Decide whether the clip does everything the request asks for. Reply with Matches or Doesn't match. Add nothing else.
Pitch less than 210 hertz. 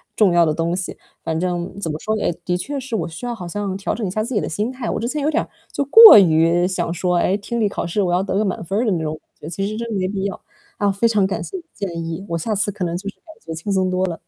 Matches